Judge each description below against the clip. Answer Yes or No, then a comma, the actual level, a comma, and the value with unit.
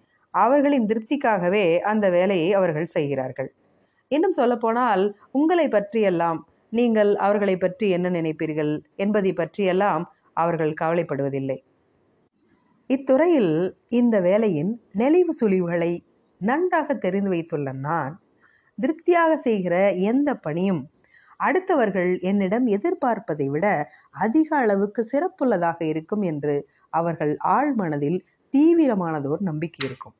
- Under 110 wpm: Yes, average, 95 wpm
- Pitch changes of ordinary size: No, wide, 6.6 semitones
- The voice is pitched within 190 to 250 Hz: Yes, high, 195 Hz